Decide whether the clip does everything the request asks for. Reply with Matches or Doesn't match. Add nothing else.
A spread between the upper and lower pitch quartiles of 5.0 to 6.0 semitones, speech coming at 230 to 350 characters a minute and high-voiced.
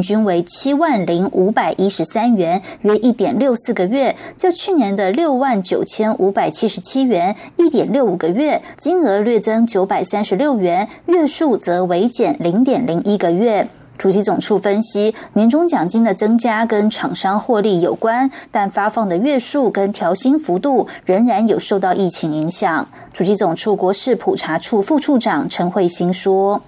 Matches